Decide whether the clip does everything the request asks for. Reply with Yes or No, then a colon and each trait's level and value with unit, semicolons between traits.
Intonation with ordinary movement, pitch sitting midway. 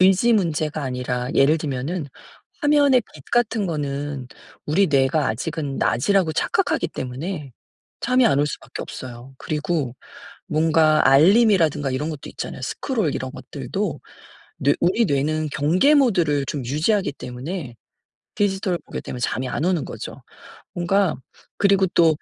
No: wide, 5.7 semitones; medium, 155 Hz